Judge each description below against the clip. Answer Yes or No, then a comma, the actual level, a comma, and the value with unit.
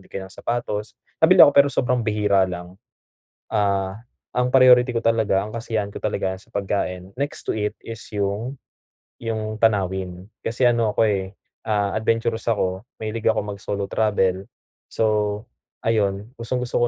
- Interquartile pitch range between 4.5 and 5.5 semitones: No, narrow, 2.6 semitones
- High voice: No, low, 105 Hz